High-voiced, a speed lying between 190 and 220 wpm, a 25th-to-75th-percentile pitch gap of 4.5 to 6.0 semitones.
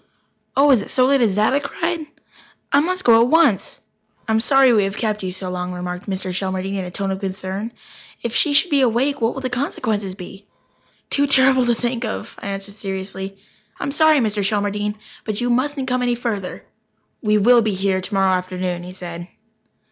Yes: high, 210 Hz; average, 200 wpm; average, 5.0 semitones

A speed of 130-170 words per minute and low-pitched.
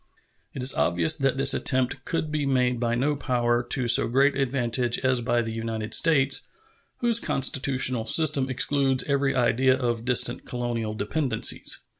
Yes: average, 155 wpm; low, 130 Hz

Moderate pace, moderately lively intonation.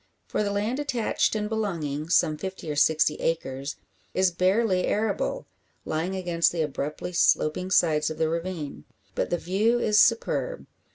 Yes: average, 155 wpm; average, 5.0 semitones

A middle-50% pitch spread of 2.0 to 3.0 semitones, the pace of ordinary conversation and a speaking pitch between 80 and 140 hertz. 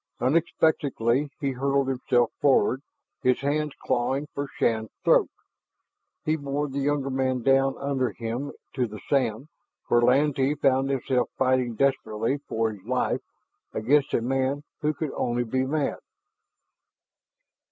No: narrow, 2.5 semitones; slow, 130 wpm; low, 135 Hz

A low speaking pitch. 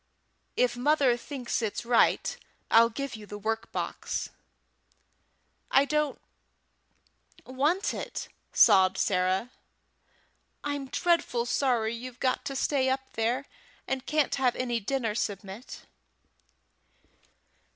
No: very high, 250 Hz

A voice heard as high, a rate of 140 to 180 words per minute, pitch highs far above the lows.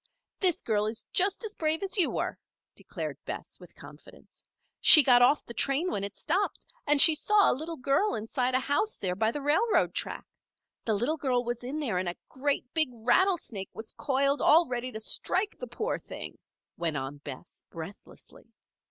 No: very high, 270 Hz; average, 190 wpm; wide, 6.7 semitones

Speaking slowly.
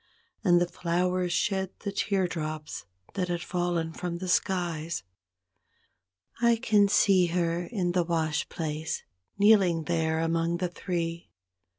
Yes: slow, 125 wpm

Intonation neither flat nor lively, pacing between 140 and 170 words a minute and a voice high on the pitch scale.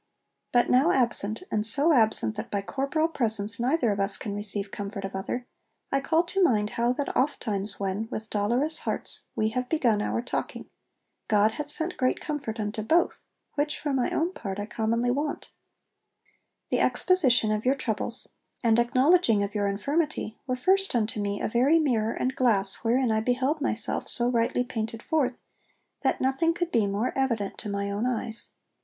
No: average, 4.6 semitones; average, 180 wpm; high, 235 Hz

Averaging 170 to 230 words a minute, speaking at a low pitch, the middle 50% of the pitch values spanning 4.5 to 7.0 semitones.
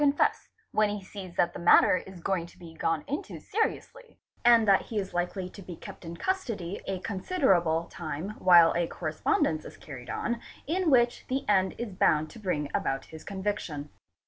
No: average, 200 wpm; high, 190 Hz; average, 5.2 semitones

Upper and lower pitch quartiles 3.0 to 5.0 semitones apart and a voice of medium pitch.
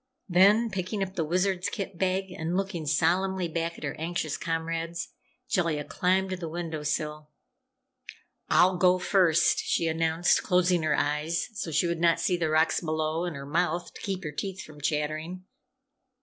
No: narrow, 2.6 semitones; medium, 170 Hz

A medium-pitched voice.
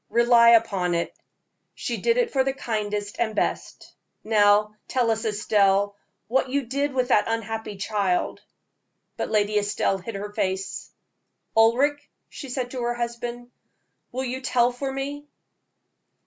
No: high, 230 Hz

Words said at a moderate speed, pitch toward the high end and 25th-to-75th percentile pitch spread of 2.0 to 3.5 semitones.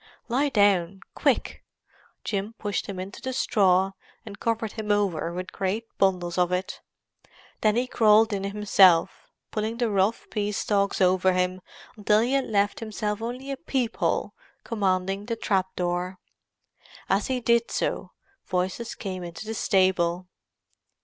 Yes: average, 145 wpm; high, 200 Hz; average, 3.2 semitones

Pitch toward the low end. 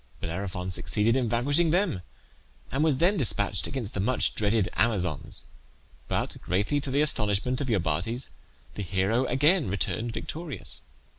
Yes: low, 115 Hz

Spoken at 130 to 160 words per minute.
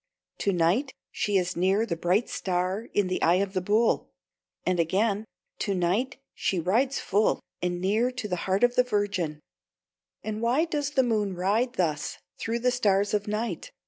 No: average, 175 wpm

